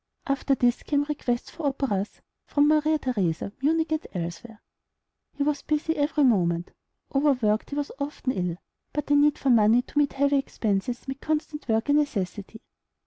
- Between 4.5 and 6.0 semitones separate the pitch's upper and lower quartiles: Yes, average, 5.2 semitones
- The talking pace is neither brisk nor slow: Yes, average, 165 wpm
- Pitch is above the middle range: Yes, very high, 275 Hz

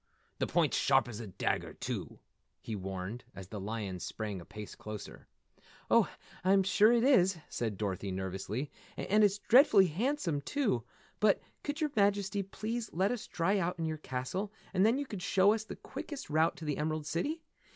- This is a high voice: No, medium, 175 Hz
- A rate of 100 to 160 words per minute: No, average, 180 wpm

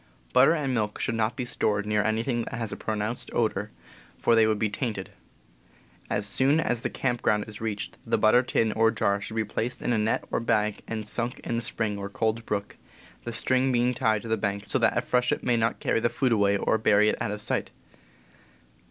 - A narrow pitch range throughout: Yes, narrow, 2.2 semitones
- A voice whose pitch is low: Yes, low, 110 Hz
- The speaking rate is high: Yes, fast, 225 wpm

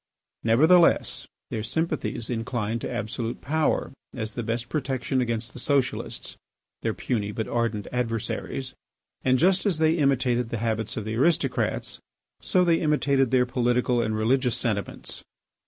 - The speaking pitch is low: Yes, low, 125 Hz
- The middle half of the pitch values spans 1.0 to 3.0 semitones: No, average, 3.4 semitones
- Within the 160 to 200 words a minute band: No, average, 140 wpm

